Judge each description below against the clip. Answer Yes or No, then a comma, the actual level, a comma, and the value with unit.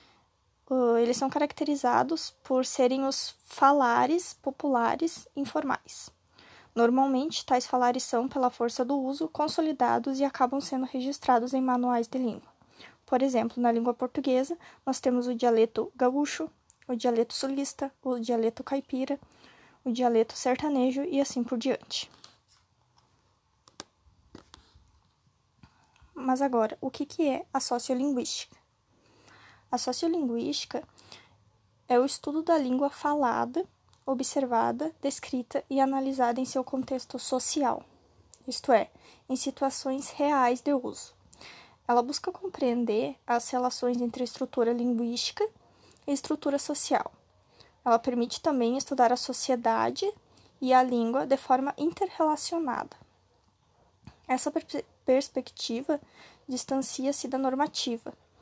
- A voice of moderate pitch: No, very high, 265 Hz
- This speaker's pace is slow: Yes, slow, 110 wpm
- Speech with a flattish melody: Yes, narrow, 2.2 semitones